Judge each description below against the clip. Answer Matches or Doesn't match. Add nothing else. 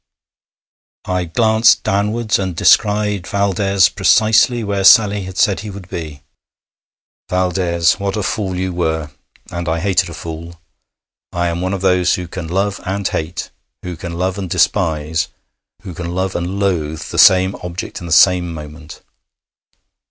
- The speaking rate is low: Doesn't match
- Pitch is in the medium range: Doesn't match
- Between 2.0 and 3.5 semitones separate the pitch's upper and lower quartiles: Matches